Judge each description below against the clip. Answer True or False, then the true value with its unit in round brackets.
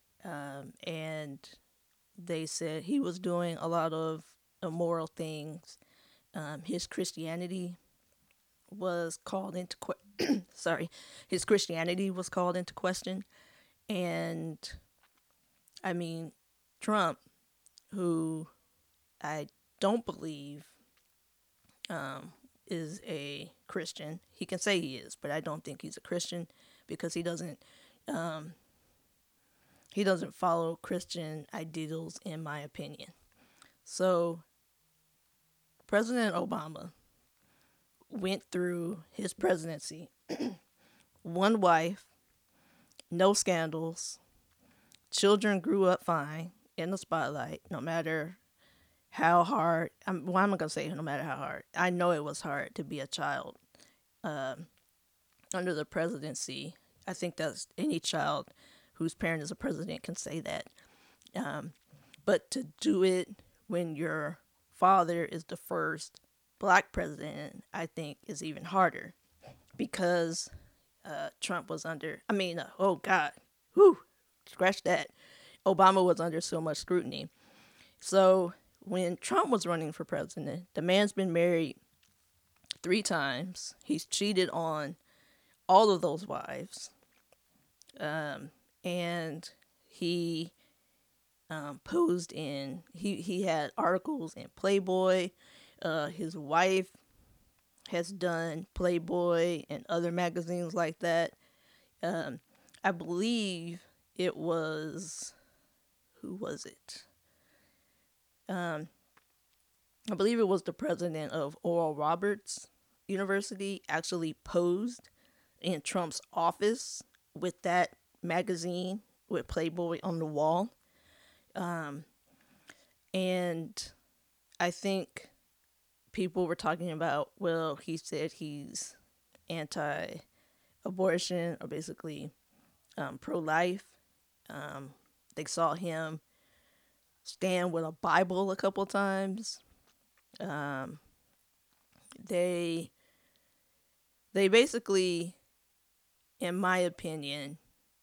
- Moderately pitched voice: True (175 Hz)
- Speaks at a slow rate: True (110 wpm)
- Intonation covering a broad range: False (2.8 semitones)